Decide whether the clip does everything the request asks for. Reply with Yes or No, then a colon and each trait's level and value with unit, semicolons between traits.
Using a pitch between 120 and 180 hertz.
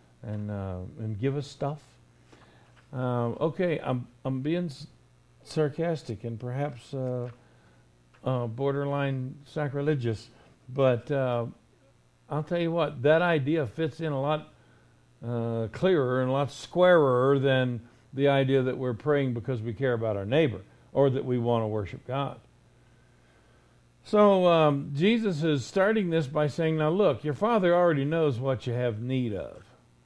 Yes: low, 135 Hz